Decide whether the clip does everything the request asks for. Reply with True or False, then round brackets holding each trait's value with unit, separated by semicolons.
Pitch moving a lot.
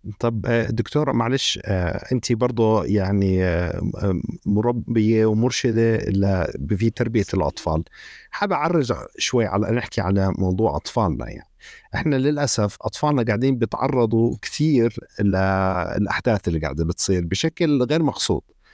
False (4.0 semitones)